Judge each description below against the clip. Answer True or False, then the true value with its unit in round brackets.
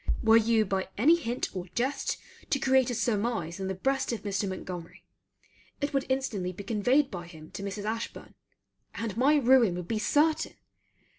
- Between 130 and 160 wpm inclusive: False (175 wpm)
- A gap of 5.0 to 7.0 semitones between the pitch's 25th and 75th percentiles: True (5.5 semitones)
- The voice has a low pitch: False (225 Hz)